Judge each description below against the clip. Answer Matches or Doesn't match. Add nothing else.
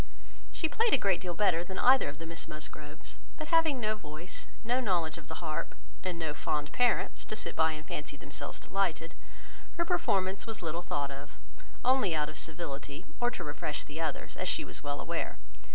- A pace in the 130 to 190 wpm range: Doesn't match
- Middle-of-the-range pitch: Matches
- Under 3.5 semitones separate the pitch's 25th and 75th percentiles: Doesn't match